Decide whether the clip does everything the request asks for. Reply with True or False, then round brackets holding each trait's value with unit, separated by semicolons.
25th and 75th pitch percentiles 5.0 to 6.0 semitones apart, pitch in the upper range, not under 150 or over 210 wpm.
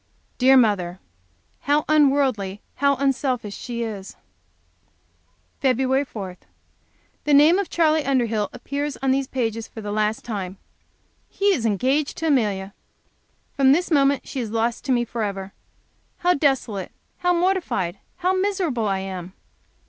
False (5.5 semitones; 255 Hz; 135 wpm)